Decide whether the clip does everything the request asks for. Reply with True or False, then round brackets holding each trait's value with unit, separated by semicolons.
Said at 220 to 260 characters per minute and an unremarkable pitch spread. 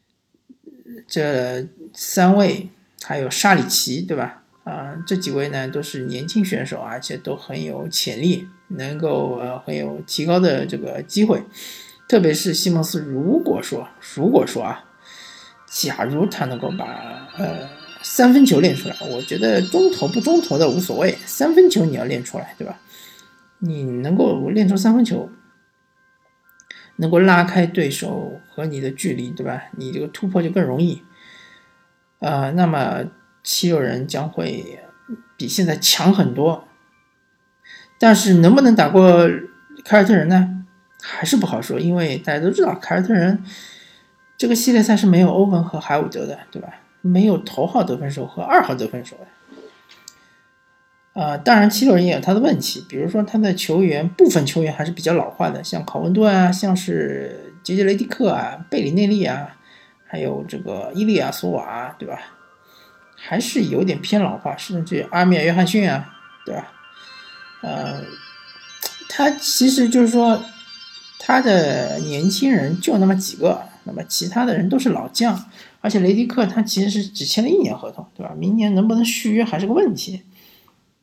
True (245 characters per minute; 3.8 semitones)